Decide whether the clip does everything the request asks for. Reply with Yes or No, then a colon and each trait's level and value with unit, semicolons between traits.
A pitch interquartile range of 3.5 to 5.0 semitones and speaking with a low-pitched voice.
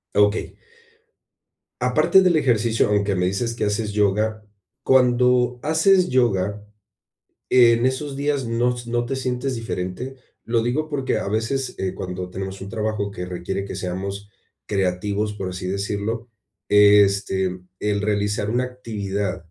Yes: average, 3.9 semitones; low, 105 Hz